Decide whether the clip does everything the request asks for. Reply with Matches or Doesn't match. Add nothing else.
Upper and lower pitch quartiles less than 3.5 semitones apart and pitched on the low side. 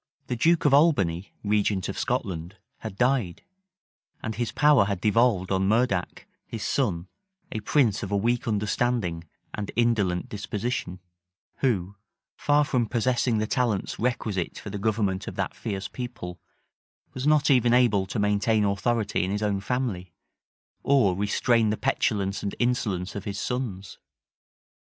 Doesn't match